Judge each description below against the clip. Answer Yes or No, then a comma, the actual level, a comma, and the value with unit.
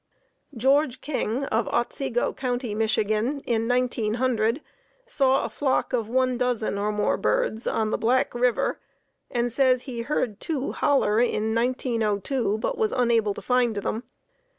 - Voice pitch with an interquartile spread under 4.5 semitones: Yes, average, 2.9 semitones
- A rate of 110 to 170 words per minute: Yes, average, 150 wpm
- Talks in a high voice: Yes, high, 240 Hz